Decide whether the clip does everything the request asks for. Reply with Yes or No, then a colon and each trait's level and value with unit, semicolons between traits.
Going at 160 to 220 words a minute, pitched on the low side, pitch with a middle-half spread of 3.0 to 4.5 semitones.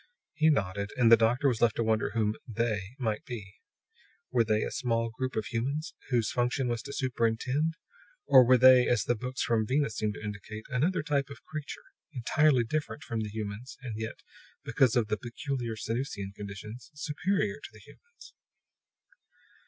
Yes: average, 175 wpm; low, 120 Hz; average, 3.9 semitones